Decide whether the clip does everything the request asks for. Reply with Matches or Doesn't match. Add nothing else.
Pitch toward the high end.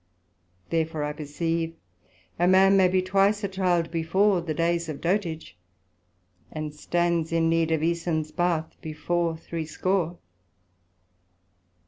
Doesn't match